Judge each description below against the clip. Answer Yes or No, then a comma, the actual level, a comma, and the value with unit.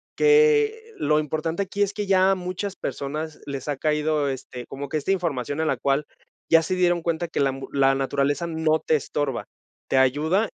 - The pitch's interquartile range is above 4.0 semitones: Yes, average, 4.8 semitones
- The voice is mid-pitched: Yes, medium, 155 Hz